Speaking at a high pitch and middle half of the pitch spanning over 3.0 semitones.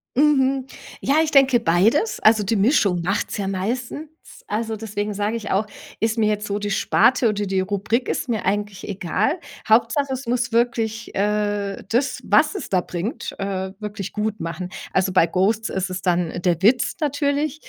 Yes: high, 210 Hz; average, 3.8 semitones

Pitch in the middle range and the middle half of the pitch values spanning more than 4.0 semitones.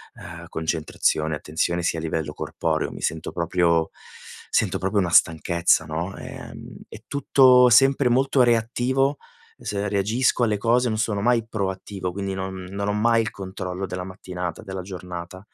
No: very low, 95 Hz; average, 4.9 semitones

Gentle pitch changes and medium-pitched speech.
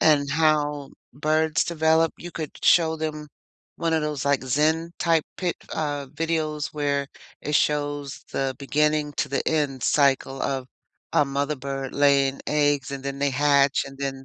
Yes: narrow, 1.9 semitones; medium, 145 Hz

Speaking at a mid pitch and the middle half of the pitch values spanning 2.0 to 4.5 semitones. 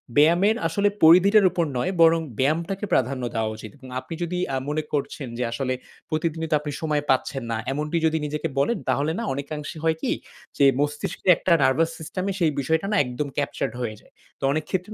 Yes: medium, 155 Hz; average, 3.6 semitones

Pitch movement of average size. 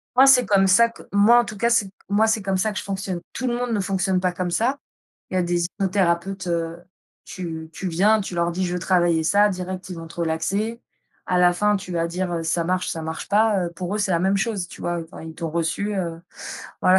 Yes: average, 3.1 semitones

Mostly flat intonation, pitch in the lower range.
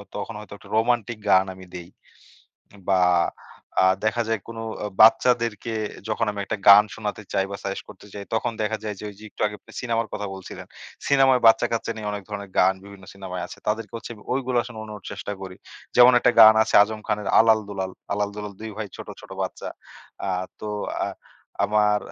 Yes: narrow, 2.1 semitones; low, 105 Hz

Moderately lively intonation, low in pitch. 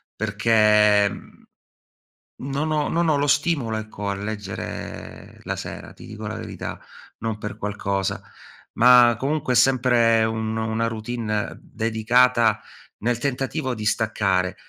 Yes: average, 3.0 semitones; low, 115 Hz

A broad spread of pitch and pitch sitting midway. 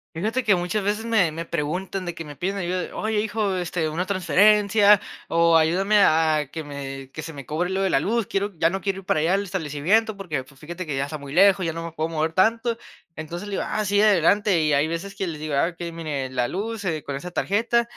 No: average, 4.4 semitones; medium, 175 Hz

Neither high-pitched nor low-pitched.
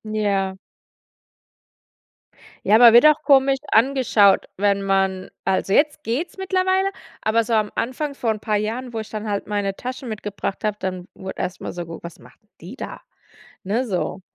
No: high, 215 Hz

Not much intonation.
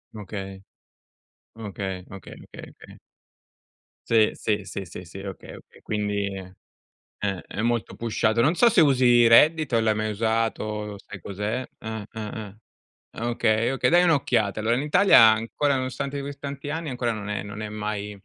No: average, 3.9 semitones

